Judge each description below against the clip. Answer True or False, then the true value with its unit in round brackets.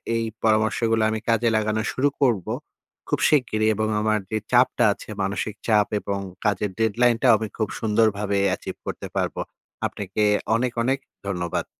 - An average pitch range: False (1.9 semitones)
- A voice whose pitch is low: True (110 Hz)